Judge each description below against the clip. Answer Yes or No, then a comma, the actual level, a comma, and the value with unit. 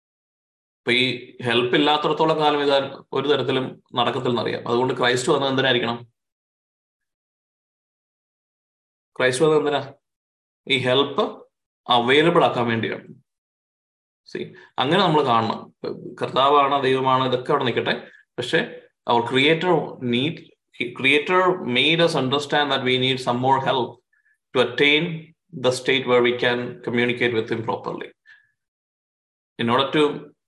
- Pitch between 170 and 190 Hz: No, low, 130 Hz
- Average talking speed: Yes, average, 85 wpm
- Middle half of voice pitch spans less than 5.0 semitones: Yes, average, 3.4 semitones